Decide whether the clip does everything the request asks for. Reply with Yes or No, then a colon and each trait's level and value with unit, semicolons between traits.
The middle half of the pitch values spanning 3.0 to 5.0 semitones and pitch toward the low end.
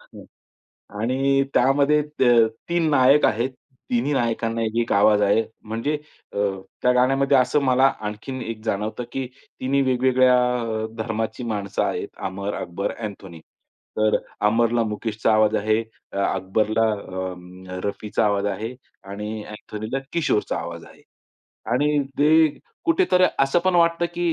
Yes: average, 4.3 semitones; low, 115 Hz